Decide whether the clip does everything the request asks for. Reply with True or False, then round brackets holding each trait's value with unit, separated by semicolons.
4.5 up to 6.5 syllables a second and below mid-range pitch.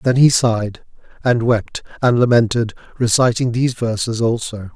True (5.0 syllables/s; 120 Hz)